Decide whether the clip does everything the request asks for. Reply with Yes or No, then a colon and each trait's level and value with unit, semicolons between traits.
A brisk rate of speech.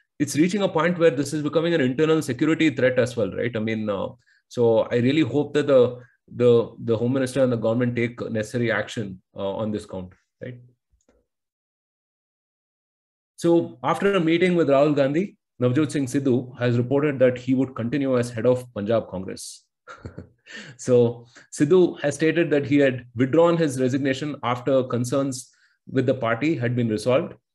No: average, 170 wpm